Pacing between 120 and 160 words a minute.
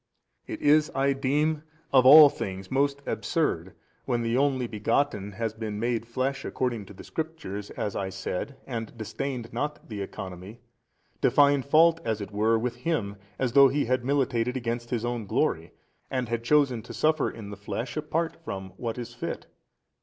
No: average, 175 wpm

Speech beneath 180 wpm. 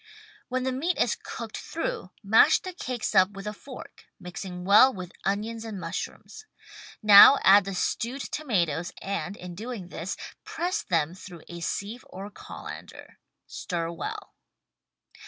Yes: average, 150 wpm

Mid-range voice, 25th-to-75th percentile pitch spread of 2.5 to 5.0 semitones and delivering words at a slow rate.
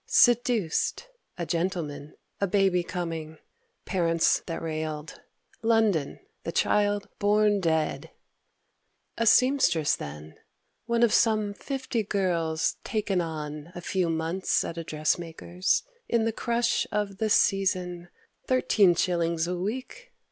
Yes: medium, 180 Hz; average, 4.5 semitones; slow, 120 wpm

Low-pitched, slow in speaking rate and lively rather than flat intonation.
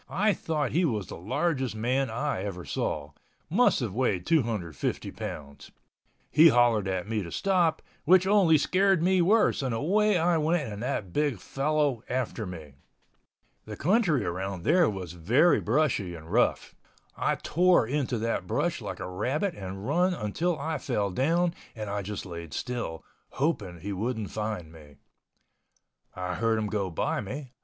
No: low, 120 Hz; average, 160 wpm; wide, 8.7 semitones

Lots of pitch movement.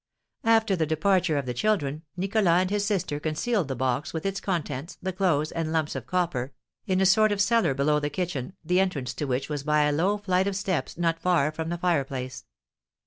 No: average, 4.6 semitones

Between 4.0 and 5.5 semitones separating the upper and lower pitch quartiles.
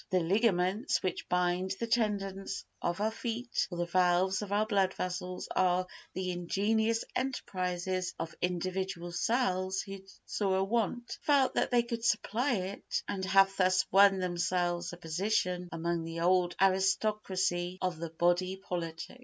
No: narrow, 2.5 semitones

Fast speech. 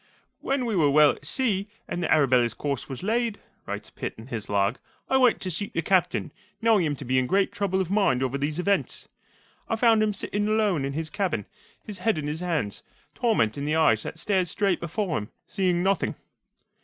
Yes: fast, 210 wpm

